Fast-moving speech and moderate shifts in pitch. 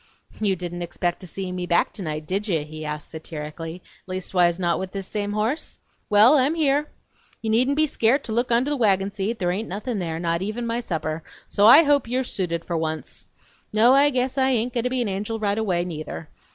No: fast, 220 wpm; wide, 5.8 semitones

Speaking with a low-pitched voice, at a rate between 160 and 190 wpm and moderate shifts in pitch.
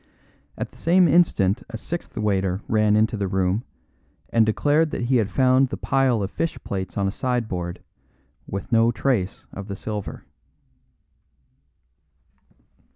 No: low, 110 Hz; average, 145 wpm; average, 4.7 semitones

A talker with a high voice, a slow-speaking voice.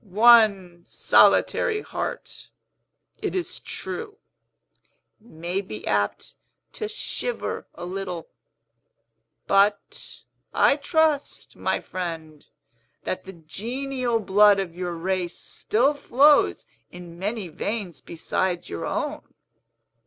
Yes: high, 195 Hz; slow, 100 wpm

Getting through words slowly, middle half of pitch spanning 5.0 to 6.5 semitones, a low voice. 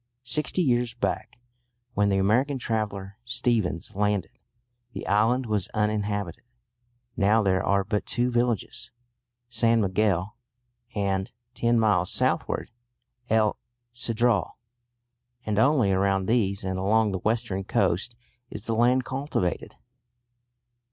No: slow, 115 wpm; average, 3.4 semitones; low, 105 Hz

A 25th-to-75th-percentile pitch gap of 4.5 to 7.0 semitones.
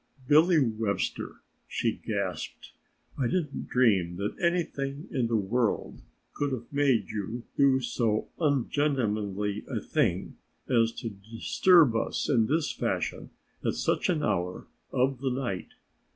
Yes: average, 4.8 semitones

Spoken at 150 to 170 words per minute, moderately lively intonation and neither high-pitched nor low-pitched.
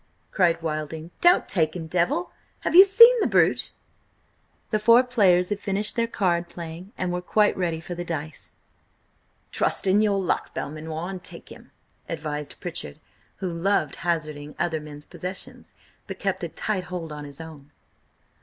Yes: average, 165 wpm; average, 4.0 semitones; medium, 175 Hz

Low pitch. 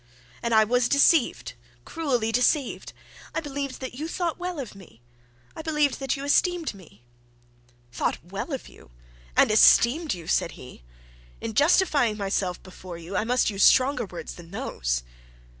No: high, 245 Hz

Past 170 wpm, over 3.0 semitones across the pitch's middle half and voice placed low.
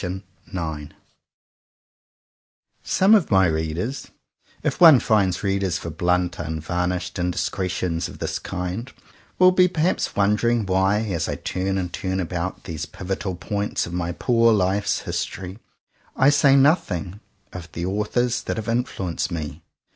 No: average, 140 wpm; average, 4.2 semitones; very low, 95 Hz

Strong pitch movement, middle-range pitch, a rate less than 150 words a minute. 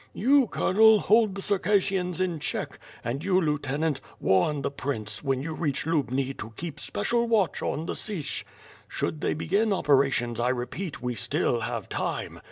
No: wide, 6.6 semitones; medium, 155 Hz; average, 160 wpm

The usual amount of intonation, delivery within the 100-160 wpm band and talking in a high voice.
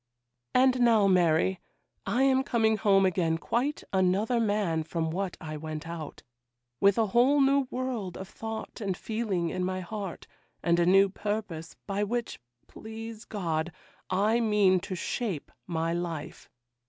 Yes: average, 4.5 semitones; average, 150 wpm; high, 195 Hz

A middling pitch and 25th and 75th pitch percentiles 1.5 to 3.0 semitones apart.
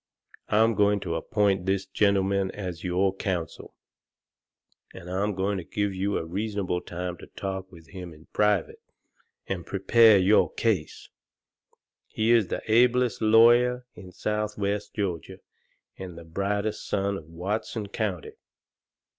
No: low, 100 Hz; average, 2.7 semitones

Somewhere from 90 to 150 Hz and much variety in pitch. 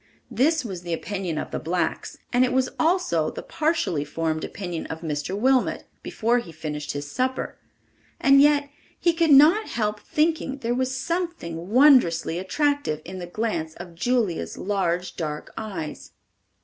No: high, 210 Hz; wide, 8.5 semitones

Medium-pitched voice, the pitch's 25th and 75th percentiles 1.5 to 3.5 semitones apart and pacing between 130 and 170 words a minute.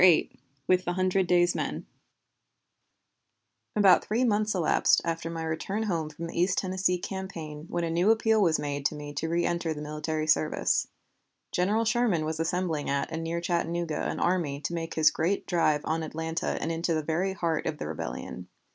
No: medium, 170 Hz; average, 2.8 semitones; average, 180 wpm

